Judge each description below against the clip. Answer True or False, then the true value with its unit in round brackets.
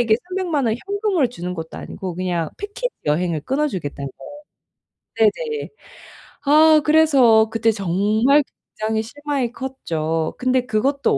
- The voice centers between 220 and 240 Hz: True (235 Hz)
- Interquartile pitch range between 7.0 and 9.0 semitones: True (8.1 semitones)